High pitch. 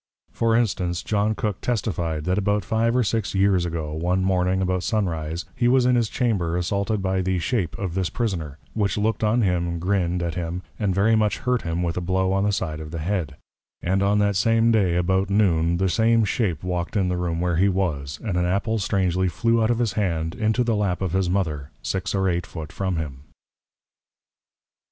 No: very low, 95 Hz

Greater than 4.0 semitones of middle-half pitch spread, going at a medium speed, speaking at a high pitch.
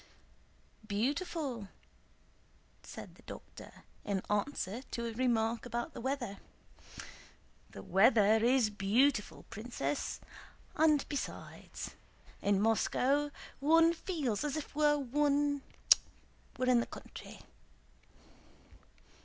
No: average, 5.1 semitones; slow, 95 wpm; high, 245 Hz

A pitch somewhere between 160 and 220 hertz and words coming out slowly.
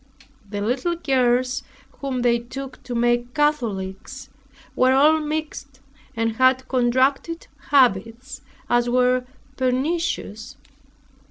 No: very high, 255 Hz; slow, 100 wpm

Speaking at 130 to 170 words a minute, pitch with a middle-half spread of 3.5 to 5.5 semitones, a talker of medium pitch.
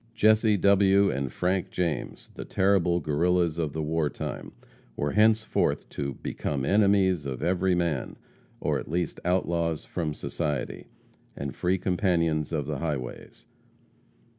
No: slow, 135 wpm; average, 4.0 semitones; very low, 85 Hz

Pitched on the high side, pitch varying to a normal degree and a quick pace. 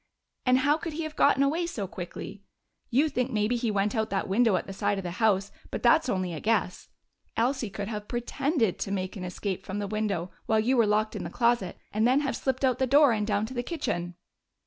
Yes: high, 220 Hz; average, 4.6 semitones; fast, 235 wpm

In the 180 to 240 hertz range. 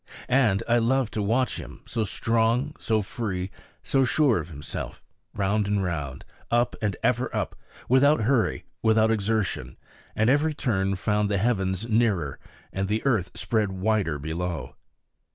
No: low, 110 Hz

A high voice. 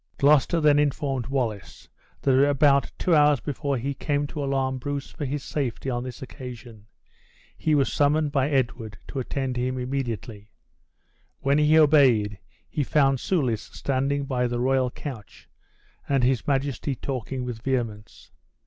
No: low, 135 Hz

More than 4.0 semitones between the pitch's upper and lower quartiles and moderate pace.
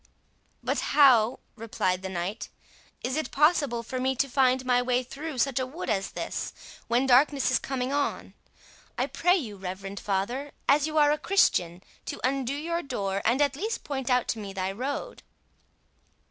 Yes: average, 4.7 semitones; average, 175 wpm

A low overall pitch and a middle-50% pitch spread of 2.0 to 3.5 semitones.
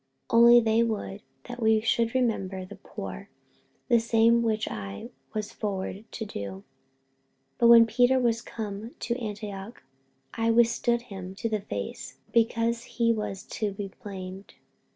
No: high, 225 Hz; average, 2.7 semitones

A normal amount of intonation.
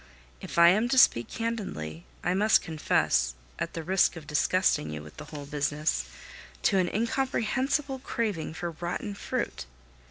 No: wide, 7.0 semitones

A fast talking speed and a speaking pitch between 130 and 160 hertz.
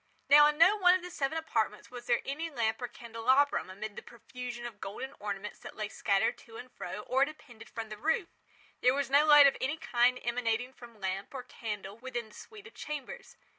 No: fast, 210 wpm; high, 245 Hz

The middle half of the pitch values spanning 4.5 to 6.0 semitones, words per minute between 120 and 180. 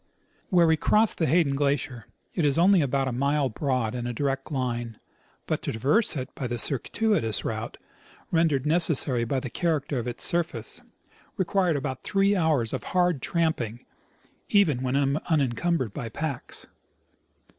Yes: average, 5.1 semitones; average, 155 wpm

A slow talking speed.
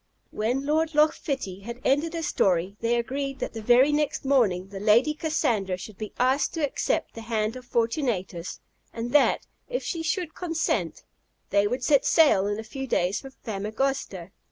No: average, 180 wpm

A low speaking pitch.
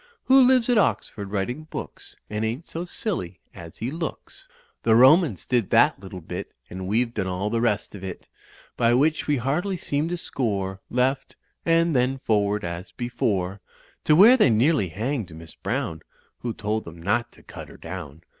Yes: low, 115 Hz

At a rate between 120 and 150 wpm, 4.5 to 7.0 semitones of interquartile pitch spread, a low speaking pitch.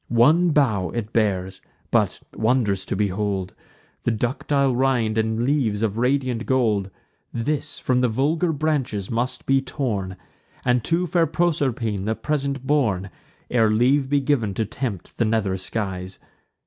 Yes: average, 145 wpm; average, 4.8 semitones; low, 120 Hz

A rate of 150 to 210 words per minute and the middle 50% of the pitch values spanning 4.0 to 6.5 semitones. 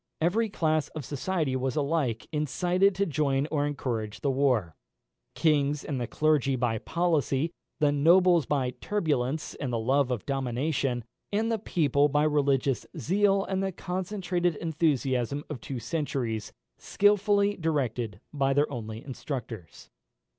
No: average, 140 wpm; average, 4.7 semitones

